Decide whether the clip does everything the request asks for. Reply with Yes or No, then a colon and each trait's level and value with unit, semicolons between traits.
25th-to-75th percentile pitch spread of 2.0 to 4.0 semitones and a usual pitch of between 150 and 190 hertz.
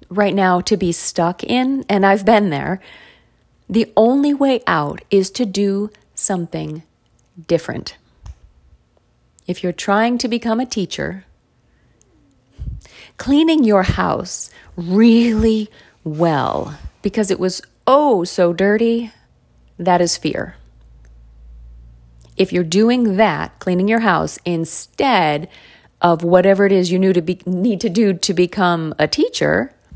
No: average, 4.6 semitones; medium, 185 Hz